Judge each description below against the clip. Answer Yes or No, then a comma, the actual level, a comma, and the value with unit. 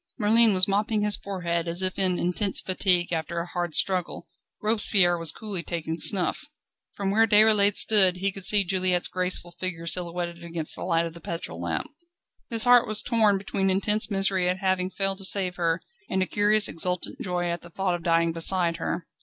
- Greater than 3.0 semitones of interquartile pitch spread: No, average, 2.7 semitones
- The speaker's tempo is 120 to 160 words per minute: No, average, 190 wpm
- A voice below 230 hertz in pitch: Yes, medium, 185 Hz